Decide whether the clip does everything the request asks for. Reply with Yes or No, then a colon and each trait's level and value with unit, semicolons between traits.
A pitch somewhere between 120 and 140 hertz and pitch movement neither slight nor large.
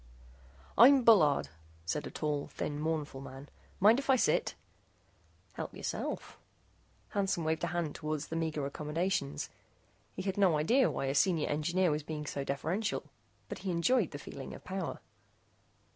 No: medium, 160 Hz; average, 4.5 semitones